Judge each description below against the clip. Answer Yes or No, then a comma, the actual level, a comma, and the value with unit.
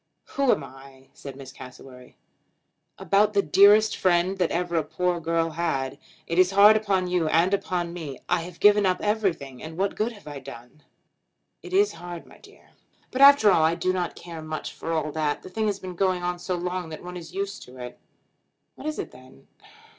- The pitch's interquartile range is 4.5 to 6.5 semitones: No, average, 3.9 semitones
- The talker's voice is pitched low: No, medium, 175 Hz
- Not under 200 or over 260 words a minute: Yes, fast, 205 wpm